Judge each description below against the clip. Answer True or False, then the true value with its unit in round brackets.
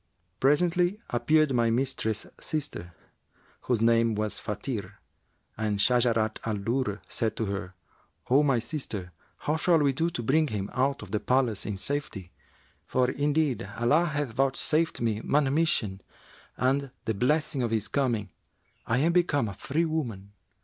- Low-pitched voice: True (125 Hz)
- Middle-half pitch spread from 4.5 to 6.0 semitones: True (5.2 semitones)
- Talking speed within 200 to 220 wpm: False (150 wpm)